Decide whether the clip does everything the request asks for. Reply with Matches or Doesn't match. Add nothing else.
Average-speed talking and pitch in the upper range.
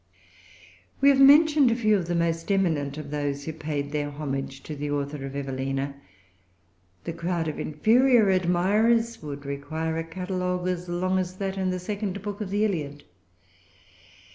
Doesn't match